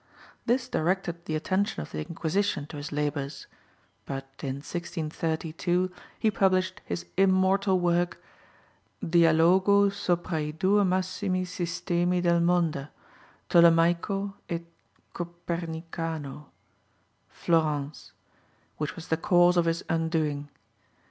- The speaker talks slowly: Yes, slow, 105 wpm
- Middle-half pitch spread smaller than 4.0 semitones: Yes, average, 2.7 semitones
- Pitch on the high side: No, medium, 170 Hz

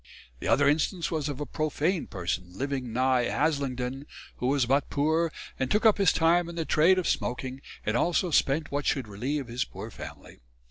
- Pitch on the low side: No, medium, 145 Hz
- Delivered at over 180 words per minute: Yes, average, 190 wpm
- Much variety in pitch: No, average, 4.2 semitones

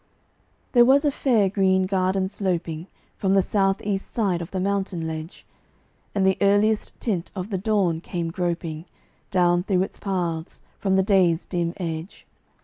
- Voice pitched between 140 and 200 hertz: Yes, high, 190 Hz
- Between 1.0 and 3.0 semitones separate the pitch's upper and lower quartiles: Yes, narrow, 2.5 semitones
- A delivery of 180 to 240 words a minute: No, average, 160 wpm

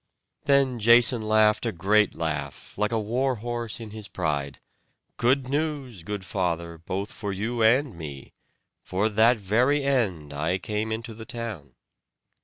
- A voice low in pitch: Yes, low, 110 Hz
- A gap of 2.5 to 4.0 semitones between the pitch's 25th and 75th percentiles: No, average, 4.4 semitones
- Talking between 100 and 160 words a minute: Yes, average, 150 wpm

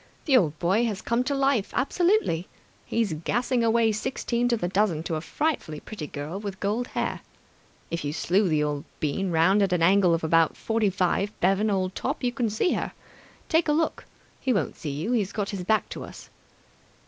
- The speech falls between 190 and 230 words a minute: Yes, average, 200 wpm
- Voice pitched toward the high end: Yes, high, 200 Hz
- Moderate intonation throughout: No, wide, 5.7 semitones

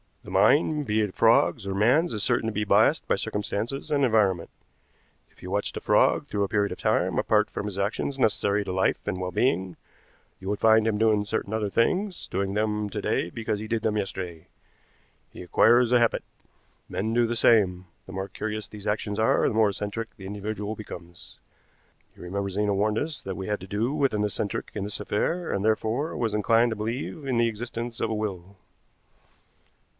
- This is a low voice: Yes, low, 105 Hz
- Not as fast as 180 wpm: No, average, 200 wpm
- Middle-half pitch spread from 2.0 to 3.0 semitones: Yes, narrow, 2.5 semitones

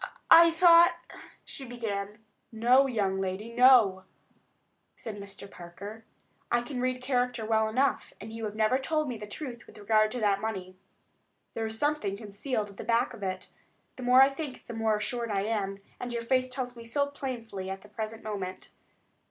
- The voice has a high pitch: Yes, high, 225 Hz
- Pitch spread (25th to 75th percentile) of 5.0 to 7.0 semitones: No, average, 3.6 semitones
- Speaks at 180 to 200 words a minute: Yes, average, 185 wpm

